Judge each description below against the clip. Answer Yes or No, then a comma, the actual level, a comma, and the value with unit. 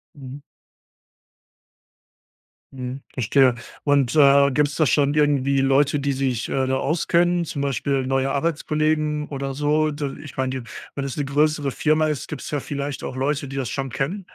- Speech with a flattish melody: Yes, narrow, 2.0 semitones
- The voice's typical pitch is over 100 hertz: Yes, medium, 140 Hz